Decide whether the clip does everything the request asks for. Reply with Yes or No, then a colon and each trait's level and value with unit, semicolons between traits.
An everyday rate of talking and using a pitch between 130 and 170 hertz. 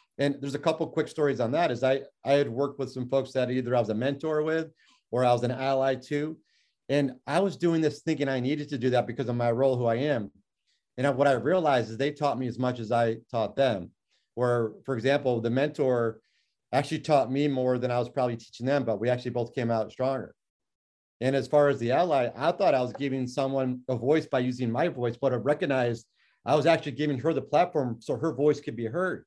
No: fast, 240 wpm; low, 135 Hz